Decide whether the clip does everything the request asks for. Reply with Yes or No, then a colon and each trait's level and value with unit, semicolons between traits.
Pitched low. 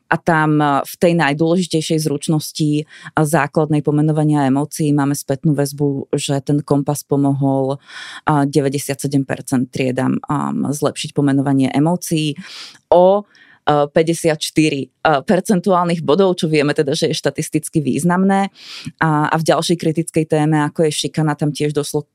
No: medium, 150 Hz